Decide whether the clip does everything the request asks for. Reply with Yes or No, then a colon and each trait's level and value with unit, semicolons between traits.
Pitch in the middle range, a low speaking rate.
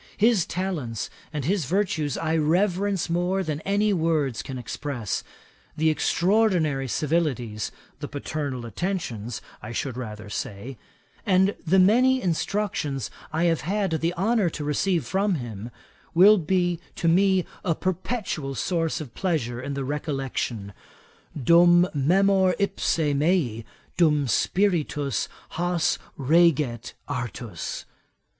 Yes: medium, 160 Hz; slow, 120 wpm